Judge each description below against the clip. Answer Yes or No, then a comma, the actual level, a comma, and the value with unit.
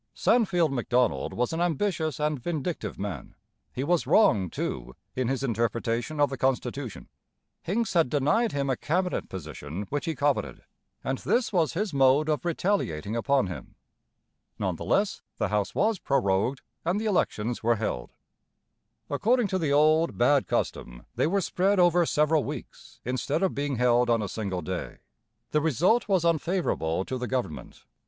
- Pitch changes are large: Yes, wide, 6.6 semitones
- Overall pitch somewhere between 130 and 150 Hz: Yes, medium, 140 Hz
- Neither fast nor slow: Yes, average, 160 wpm